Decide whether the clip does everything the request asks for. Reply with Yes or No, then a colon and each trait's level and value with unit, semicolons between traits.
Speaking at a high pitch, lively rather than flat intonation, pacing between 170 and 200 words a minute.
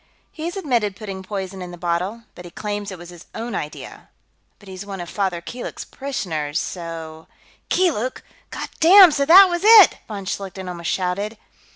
Yes: high, 195 Hz; wide, 6.0 semitones; average, 175 wpm